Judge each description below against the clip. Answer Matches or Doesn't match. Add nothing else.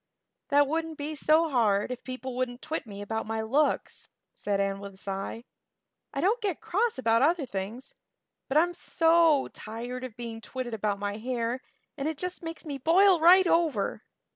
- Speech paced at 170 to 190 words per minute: Matches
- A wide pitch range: Matches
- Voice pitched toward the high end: Matches